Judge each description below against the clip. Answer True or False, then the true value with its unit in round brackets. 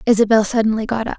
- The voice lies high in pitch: True (220 Hz)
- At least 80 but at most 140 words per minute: False (205 wpm)